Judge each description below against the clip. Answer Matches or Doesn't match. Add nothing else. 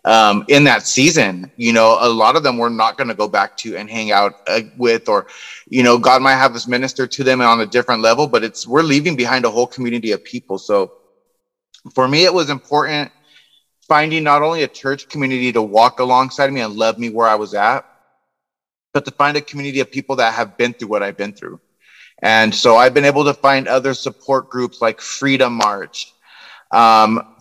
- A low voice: Matches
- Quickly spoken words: Matches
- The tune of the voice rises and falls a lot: Doesn't match